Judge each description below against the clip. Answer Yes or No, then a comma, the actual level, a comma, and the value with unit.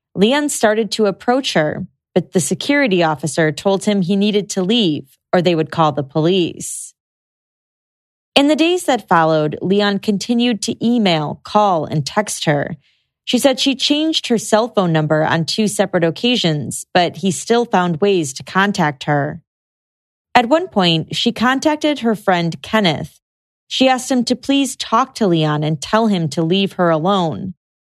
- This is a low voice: No, high, 195 Hz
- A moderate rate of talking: Yes, average, 165 wpm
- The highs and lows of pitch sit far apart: Yes, wide, 6.2 semitones